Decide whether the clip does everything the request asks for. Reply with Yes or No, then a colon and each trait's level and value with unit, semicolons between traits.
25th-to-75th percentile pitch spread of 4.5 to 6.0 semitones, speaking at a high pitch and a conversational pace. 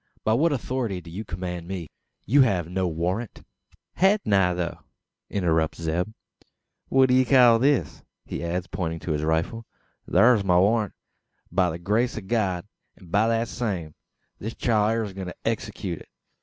No: average, 4.8 semitones; very low, 95 Hz; average, 170 wpm